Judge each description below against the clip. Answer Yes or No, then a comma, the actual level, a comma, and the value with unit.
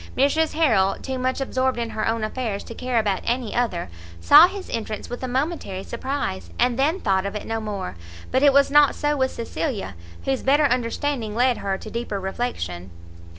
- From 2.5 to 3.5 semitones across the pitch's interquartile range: No, average, 4.4 semitones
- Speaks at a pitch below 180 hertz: No, high, 245 Hz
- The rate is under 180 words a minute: No, average, 195 wpm